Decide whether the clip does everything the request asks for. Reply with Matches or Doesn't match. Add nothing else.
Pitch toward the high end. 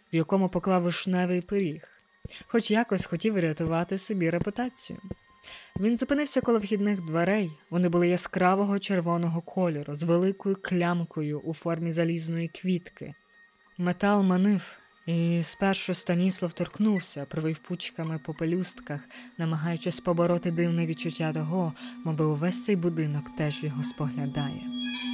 Doesn't match